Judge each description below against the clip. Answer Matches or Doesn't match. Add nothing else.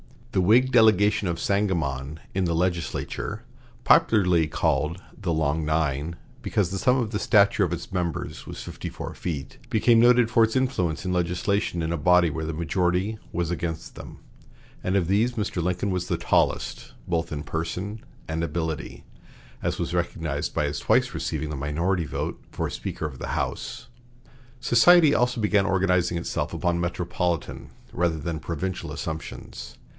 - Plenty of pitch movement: Doesn't match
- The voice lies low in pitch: Matches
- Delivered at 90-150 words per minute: Doesn't match